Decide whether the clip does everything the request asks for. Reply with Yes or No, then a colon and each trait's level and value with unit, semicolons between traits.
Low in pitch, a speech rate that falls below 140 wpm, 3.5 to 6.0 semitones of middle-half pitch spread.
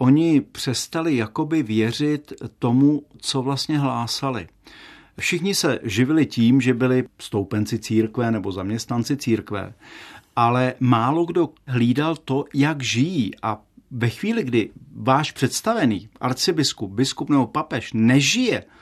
Yes: low, 130 Hz; average, 120 wpm; average, 4.1 semitones